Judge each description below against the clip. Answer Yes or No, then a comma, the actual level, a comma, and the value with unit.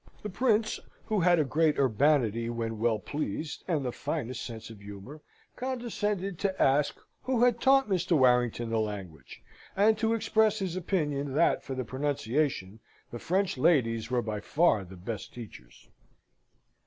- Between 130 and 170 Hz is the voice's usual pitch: Yes, medium, 140 Hz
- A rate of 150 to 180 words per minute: Yes, average, 155 wpm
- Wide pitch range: Yes, wide, 8.7 semitones